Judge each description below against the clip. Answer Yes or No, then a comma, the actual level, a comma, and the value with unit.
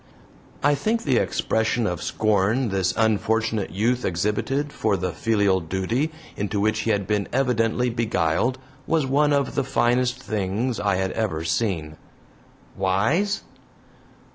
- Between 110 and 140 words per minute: Yes, slow, 135 wpm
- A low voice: Yes, low, 110 Hz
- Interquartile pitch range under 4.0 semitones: No, average, 4.6 semitones